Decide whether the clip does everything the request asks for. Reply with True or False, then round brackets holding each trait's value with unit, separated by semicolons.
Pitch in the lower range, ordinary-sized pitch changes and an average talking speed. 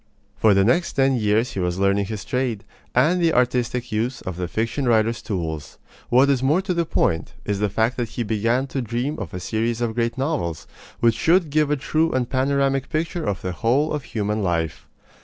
False (120 Hz; 4.8 semitones; 210 wpm)